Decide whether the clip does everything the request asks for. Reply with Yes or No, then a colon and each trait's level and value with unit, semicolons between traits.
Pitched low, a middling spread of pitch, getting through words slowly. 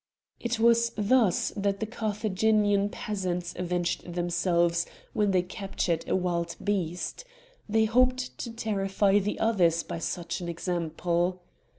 No: high, 195 Hz; average, 3.8 semitones; slow, 125 wpm